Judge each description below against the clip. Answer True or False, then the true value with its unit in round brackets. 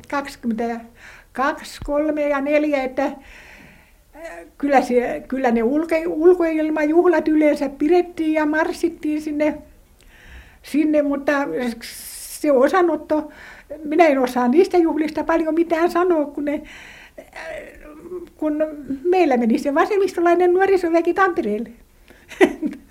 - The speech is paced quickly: False (95 wpm)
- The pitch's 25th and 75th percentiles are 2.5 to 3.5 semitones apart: True (3.0 semitones)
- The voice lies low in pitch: False (305 Hz)